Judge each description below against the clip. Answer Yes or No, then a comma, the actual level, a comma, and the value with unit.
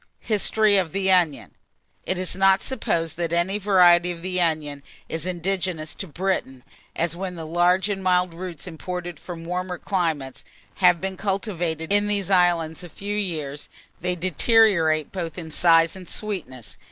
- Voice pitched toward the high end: No, medium, 180 Hz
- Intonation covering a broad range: No, narrow, 2.6 semitones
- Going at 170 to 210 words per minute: No, average, 160 wpm